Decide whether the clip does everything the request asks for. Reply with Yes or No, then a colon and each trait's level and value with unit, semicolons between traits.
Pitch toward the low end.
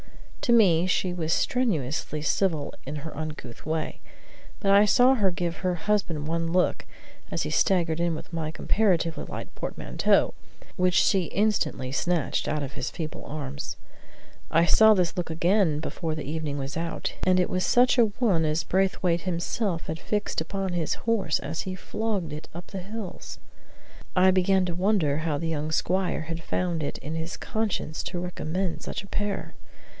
No: medium, 175 Hz